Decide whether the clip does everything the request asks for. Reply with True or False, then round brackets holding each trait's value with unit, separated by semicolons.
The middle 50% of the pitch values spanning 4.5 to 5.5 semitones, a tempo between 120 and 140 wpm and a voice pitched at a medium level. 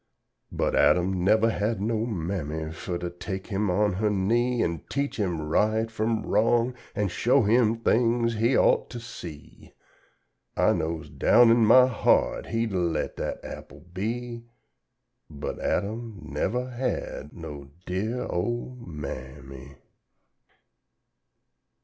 False (5.1 semitones; 135 wpm; 105 Hz)